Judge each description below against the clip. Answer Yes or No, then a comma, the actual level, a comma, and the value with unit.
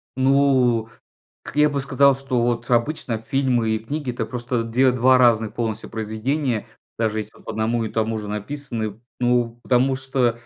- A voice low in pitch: Yes, low, 120 Hz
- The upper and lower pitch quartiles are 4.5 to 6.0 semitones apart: No, average, 2.9 semitones